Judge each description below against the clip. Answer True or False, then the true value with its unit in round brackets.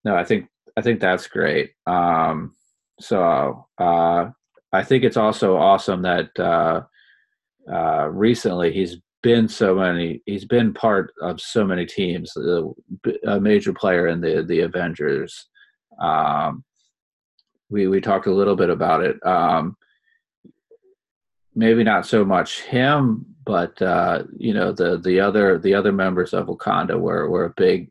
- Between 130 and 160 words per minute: True (150 wpm)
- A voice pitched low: True (105 Hz)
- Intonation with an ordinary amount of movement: False (6.3 semitones)